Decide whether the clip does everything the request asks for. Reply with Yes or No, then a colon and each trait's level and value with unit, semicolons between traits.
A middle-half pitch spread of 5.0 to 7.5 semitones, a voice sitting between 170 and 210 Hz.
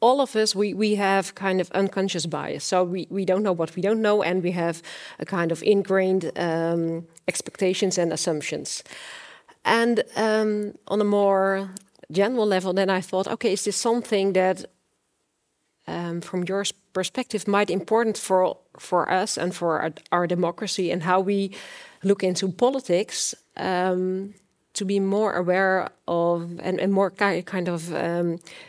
No: narrow, 2.4 semitones; high, 190 Hz